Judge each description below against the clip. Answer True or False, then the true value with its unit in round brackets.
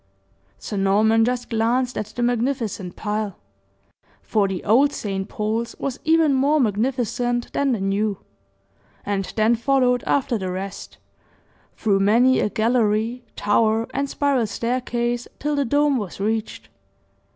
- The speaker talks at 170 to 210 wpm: False (135 wpm)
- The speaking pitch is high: True (230 Hz)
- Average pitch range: True (3.3 semitones)